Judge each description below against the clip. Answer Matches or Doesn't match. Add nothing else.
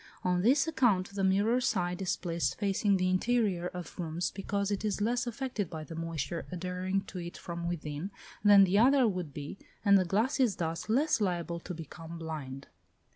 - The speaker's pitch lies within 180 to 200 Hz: Matches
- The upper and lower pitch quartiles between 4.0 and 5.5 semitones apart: Doesn't match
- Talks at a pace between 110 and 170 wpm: Doesn't match